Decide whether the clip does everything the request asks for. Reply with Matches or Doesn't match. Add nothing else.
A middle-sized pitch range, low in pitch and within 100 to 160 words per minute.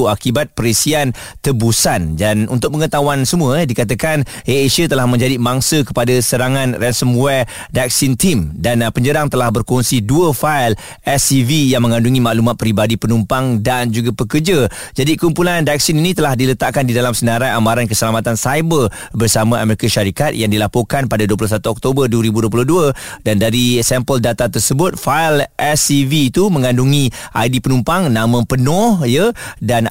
Matches